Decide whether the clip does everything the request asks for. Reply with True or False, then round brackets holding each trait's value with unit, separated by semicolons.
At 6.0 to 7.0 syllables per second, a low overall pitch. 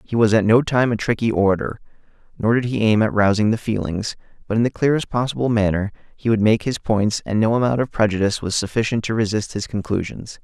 True (6.1 syllables/s; 110 Hz)